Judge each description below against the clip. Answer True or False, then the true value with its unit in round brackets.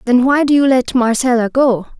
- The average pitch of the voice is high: True (255 Hz)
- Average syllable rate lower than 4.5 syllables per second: False (5.1 syllables/s)